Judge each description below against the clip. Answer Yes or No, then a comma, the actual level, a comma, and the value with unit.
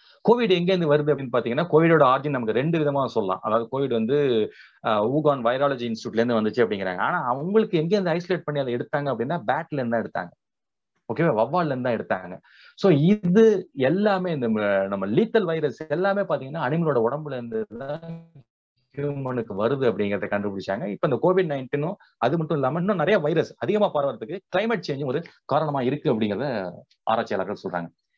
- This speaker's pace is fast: Yes, fast, 150 wpm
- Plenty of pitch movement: Yes, wide, 6.2 semitones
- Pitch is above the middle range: No, medium, 145 Hz